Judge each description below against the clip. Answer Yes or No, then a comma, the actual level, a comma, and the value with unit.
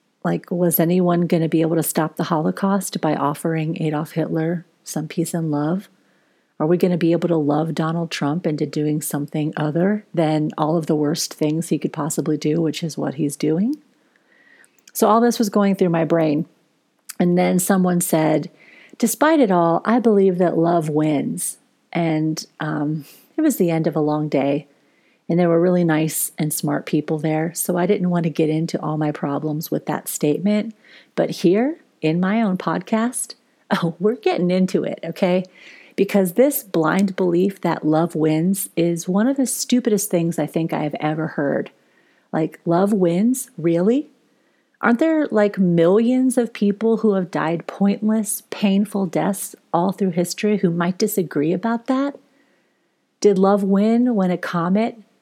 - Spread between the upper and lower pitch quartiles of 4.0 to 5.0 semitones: Yes, average, 4.7 semitones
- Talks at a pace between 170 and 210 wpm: Yes, average, 175 wpm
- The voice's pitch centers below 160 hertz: No, medium, 175 Hz